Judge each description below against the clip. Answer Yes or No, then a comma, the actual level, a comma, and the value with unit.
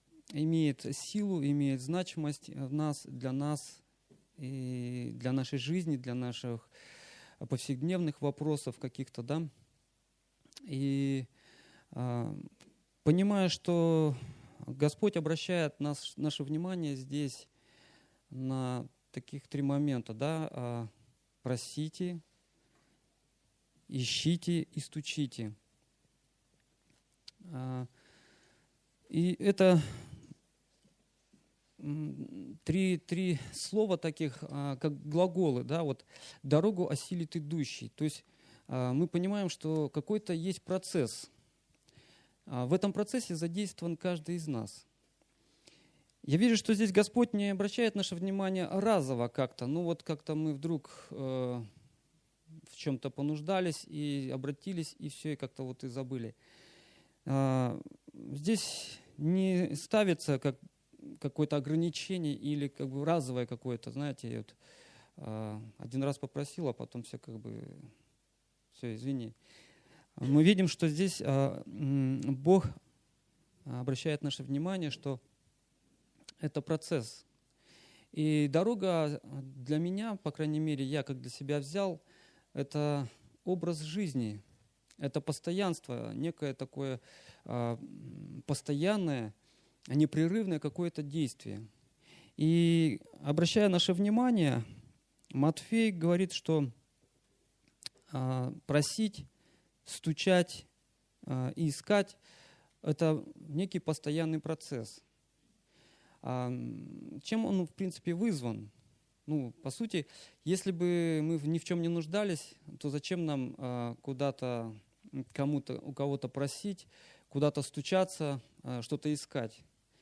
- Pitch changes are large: No, average, 4.4 semitones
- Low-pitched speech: No, medium, 150 Hz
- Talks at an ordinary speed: No, slow, 100 wpm